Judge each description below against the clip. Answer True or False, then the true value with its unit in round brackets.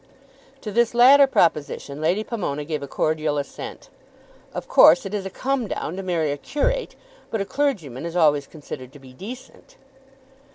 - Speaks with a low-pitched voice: False (175 Hz)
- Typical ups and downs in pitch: False (8.0 semitones)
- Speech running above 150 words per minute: True (170 wpm)